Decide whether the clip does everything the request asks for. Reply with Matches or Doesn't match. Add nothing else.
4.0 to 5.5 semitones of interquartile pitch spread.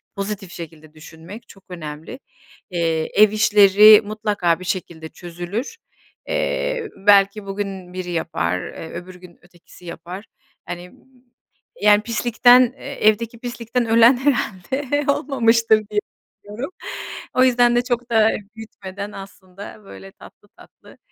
Matches